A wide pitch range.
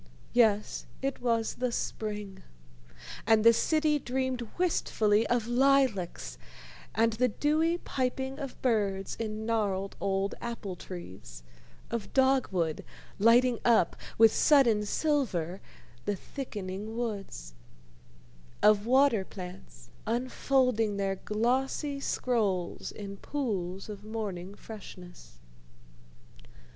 No: average, 4.4 semitones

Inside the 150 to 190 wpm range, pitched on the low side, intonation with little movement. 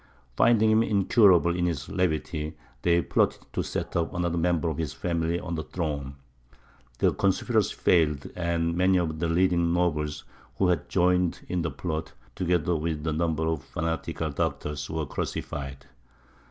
Yes: average, 155 wpm; very low, 85 Hz; narrow, 2.1 semitones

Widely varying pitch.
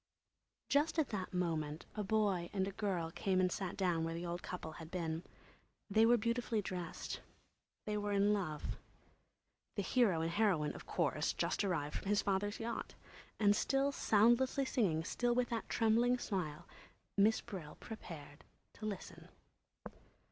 No: average, 4.6 semitones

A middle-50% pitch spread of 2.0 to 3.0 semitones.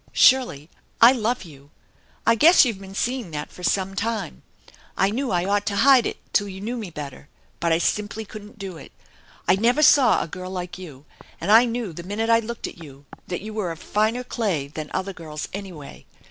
No: average, 5.1 semitones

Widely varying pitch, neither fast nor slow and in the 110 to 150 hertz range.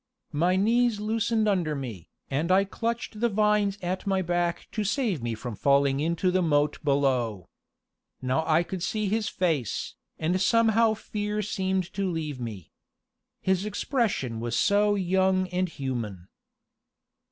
No: wide, 6.8 semitones; average, 145 wpm; medium, 185 Hz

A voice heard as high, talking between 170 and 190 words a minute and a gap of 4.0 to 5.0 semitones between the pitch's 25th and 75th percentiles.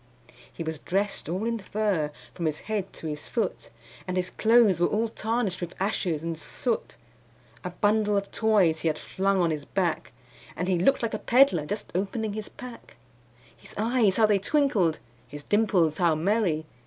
Yes: high, 195 Hz; average, 180 wpm; average, 4.6 semitones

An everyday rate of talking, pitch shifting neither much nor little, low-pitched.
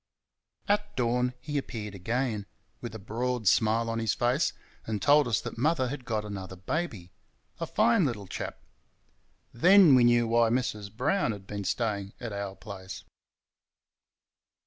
Yes: average, 150 wpm; average, 4.0 semitones; low, 115 Hz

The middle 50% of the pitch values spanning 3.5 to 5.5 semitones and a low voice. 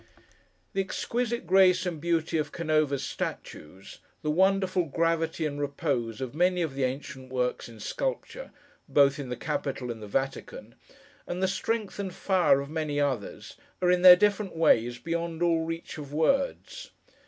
No: average, 4.8 semitones; medium, 160 Hz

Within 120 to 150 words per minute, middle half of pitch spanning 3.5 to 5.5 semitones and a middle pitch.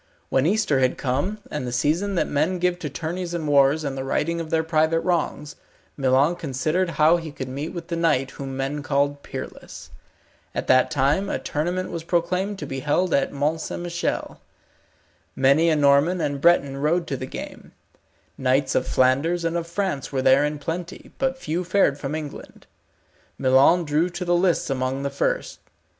No: average, 185 wpm; average, 3.9 semitones; medium, 155 Hz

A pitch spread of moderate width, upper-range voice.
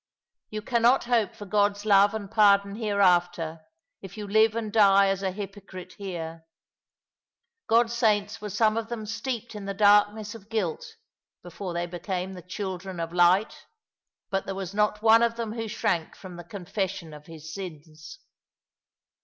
Yes: average, 3.2 semitones; high, 200 Hz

